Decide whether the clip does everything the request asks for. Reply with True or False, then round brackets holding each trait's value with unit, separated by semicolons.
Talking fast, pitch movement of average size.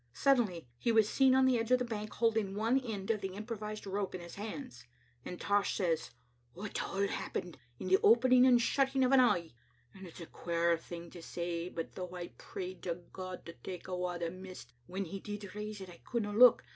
True (220 wpm; 4.4 semitones)